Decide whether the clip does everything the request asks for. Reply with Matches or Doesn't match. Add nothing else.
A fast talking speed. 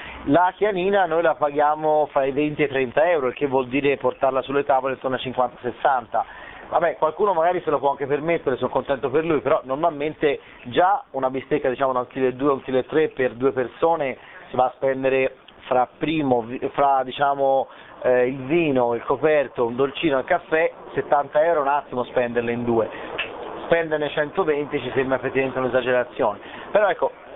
Matches